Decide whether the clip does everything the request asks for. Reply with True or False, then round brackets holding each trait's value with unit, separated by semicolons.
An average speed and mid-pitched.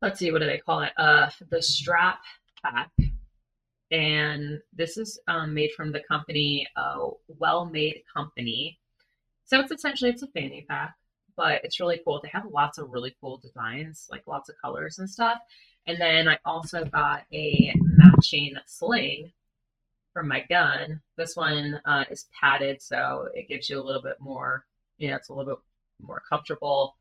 True (180 wpm; 155 Hz)